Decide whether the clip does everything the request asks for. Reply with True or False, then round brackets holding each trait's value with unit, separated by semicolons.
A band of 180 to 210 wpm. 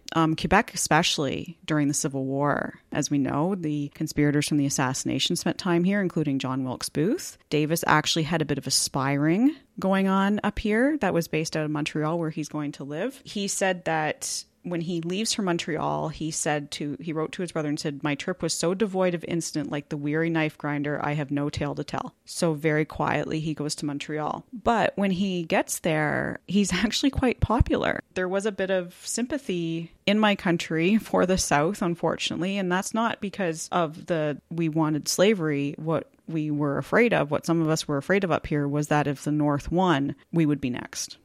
True (205 wpm)